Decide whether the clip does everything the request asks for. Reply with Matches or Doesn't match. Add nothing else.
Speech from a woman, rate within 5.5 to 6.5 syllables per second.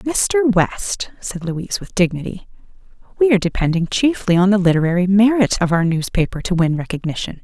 Matches